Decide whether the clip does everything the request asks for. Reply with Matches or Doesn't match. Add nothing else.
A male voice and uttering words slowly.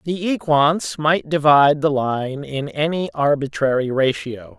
Matches